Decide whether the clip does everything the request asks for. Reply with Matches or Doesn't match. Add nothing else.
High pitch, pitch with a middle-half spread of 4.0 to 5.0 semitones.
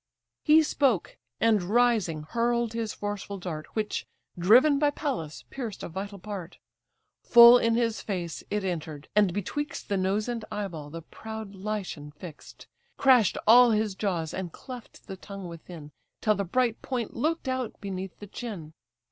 Matches